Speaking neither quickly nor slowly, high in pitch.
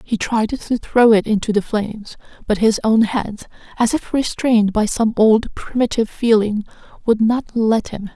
Yes: average, 175 wpm; high, 220 Hz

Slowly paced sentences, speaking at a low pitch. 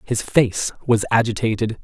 Yes: slow, 130 wpm; low, 115 Hz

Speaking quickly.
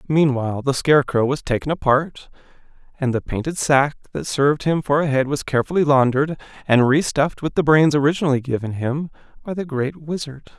No: average, 175 wpm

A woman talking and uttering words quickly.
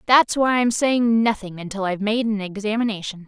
No: female; average, 185 wpm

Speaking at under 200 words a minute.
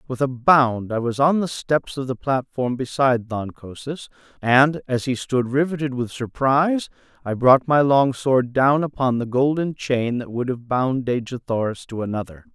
Yes: average, 185 wpm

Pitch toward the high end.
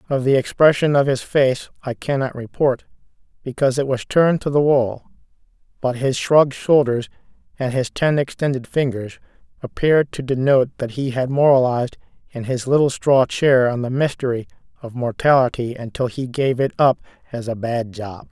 No: low, 130 Hz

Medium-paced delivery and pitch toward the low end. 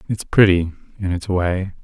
Yes: average, 165 wpm; very low, 95 Hz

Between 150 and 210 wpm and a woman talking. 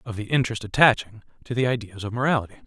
No: average, 200 wpm; male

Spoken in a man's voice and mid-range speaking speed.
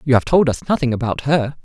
No: male; fast, 255 wpm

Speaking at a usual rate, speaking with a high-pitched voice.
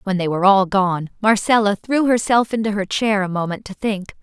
No: fast, 215 wpm; high, 205 Hz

